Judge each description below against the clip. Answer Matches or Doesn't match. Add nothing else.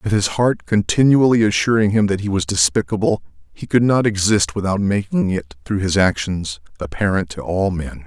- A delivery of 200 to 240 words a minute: Doesn't match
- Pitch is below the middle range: Matches